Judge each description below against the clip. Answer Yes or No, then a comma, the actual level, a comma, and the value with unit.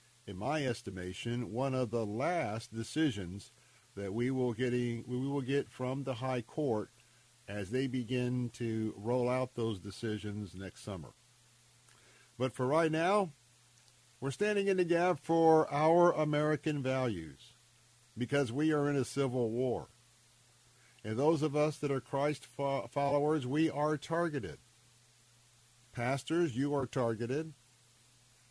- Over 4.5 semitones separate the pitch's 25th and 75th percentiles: No, average, 3.1 semitones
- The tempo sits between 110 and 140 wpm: Yes, slow, 135 wpm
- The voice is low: Yes, low, 125 Hz